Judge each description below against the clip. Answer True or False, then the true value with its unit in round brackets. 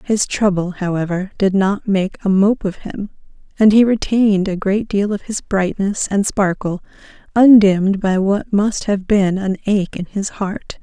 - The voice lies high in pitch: True (200 Hz)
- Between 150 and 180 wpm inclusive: True (175 wpm)